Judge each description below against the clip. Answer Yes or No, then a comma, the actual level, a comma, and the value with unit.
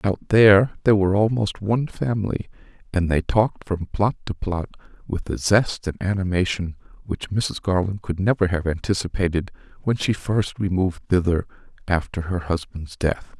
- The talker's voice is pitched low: Yes, very low, 95 Hz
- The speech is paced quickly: No, average, 155 wpm